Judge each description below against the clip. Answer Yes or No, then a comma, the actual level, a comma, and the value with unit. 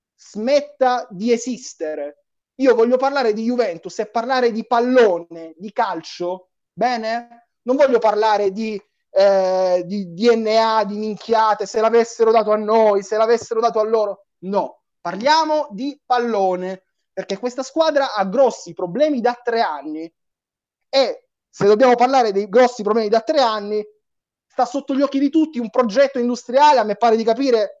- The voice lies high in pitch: Yes, high, 225 Hz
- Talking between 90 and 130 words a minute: No, average, 155 wpm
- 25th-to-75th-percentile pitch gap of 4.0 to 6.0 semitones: No, average, 3.6 semitones